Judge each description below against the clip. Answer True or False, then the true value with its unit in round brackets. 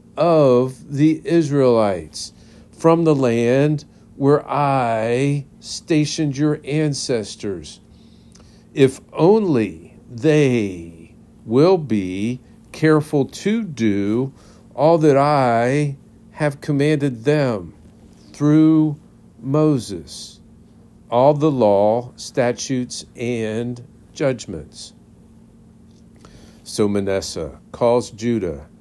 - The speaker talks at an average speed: False (75 wpm)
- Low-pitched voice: True (130 Hz)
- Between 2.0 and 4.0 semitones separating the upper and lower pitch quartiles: False (4.7 semitones)